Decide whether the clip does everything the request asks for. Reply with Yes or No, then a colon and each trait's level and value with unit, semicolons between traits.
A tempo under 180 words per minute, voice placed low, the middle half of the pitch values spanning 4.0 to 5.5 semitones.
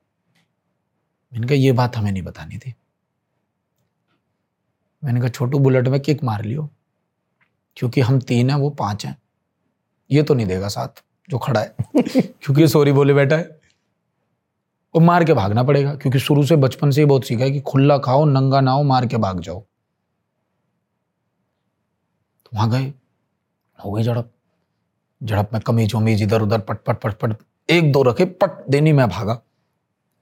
Yes: average, 150 wpm; low, 130 Hz; average, 4.4 semitones